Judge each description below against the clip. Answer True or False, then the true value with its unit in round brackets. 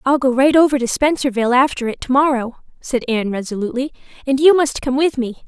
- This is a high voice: True (260 Hz)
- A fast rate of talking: False (195 wpm)